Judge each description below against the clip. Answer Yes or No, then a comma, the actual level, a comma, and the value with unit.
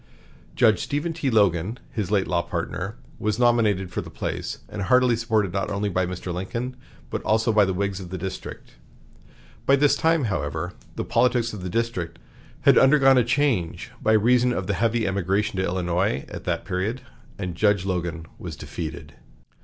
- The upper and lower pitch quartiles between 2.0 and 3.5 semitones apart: No, average, 4.5 semitones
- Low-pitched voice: Yes, low, 105 Hz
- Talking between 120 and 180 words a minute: Yes, average, 175 wpm